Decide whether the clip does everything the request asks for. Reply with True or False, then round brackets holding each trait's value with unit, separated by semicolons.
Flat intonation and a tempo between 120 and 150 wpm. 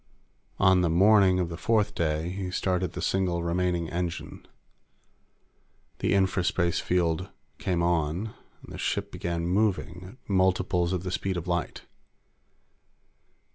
True (1.7 semitones; 135 wpm)